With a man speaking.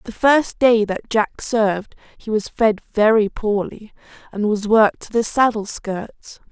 No: female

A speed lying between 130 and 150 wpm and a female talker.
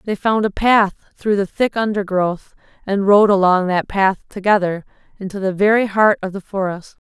No: average, 180 wpm; female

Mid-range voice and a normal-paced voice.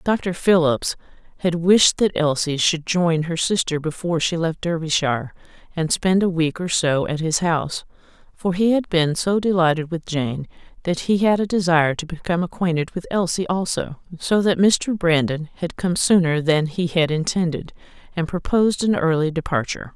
Yes: medium, 170 Hz; average, 175 wpm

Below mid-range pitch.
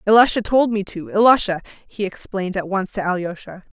No: high, 200 Hz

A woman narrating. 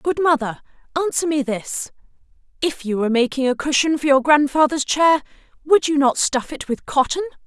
Yes: female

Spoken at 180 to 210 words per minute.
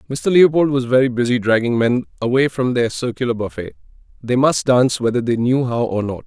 Yes: average, 190 wpm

